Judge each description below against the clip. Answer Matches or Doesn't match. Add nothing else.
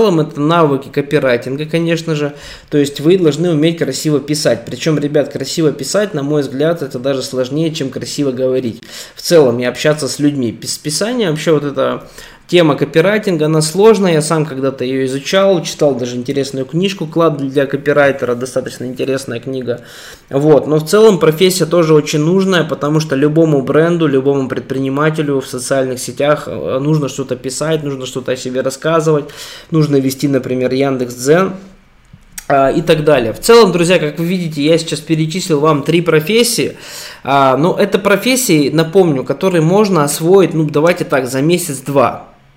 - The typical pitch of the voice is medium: Matches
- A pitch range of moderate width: Matches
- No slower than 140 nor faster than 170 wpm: Matches